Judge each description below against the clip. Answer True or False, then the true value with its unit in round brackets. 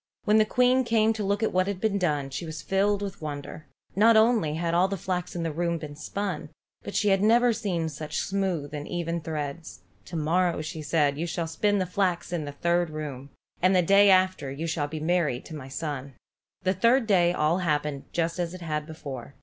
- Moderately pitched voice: True (170 Hz)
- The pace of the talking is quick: True (225 wpm)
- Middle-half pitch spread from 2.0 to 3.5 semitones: False (4.3 semitones)